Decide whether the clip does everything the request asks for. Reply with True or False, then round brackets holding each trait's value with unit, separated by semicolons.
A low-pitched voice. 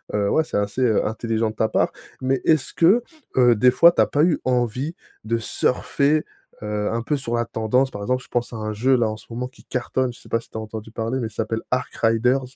True (120 Hz)